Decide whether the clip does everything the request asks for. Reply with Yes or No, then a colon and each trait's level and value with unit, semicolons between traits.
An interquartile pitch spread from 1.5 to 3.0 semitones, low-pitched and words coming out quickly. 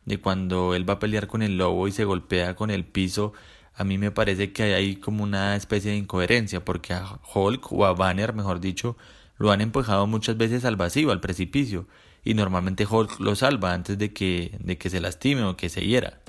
Yes: narrow, 2.6 semitones; low, 100 Hz; fast, 215 wpm